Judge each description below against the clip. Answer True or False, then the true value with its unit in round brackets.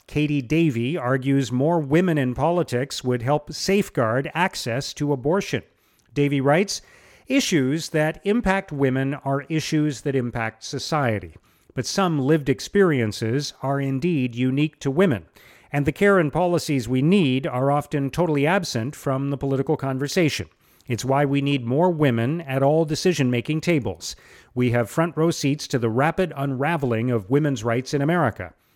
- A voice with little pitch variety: False (3.7 semitones)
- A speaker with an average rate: True (150 wpm)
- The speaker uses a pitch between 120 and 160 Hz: True (140 Hz)